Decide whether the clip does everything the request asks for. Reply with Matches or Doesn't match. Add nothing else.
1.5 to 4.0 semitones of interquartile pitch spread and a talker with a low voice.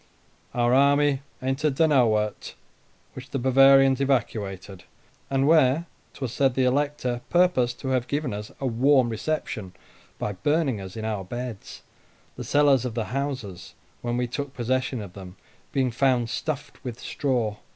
Matches